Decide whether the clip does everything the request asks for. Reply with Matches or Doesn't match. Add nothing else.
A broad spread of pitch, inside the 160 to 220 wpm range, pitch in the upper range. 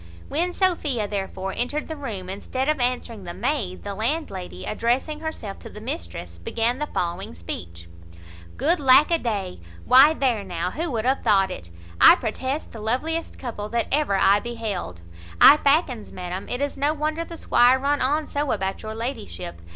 Matches